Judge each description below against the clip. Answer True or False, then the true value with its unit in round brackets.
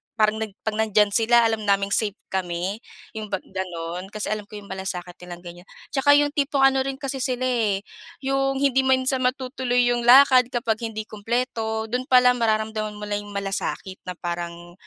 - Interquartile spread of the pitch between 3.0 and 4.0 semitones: False (4.4 semitones)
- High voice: True (220 Hz)